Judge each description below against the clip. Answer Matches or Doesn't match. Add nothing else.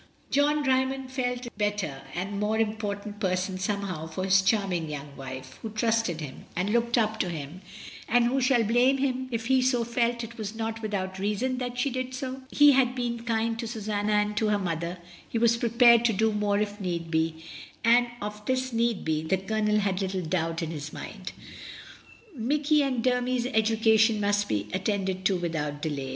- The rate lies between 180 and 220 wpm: Matches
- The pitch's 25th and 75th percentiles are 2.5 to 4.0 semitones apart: Doesn't match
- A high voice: Matches